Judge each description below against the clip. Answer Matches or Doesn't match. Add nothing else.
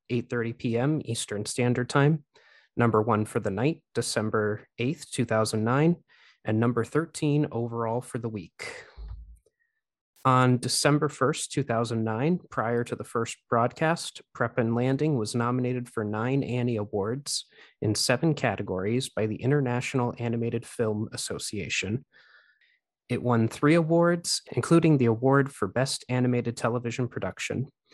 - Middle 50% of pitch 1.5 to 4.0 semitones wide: Matches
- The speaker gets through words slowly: Matches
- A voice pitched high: Doesn't match